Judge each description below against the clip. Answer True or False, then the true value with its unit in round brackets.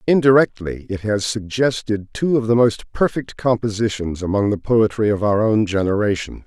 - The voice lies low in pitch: True (110 Hz)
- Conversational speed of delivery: True (160 wpm)